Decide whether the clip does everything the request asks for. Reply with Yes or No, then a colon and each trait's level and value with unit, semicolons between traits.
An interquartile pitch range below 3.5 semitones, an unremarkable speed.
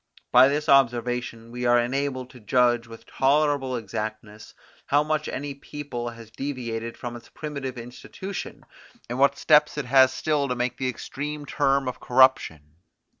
Yes: average, 2.9 semitones; average, 160 wpm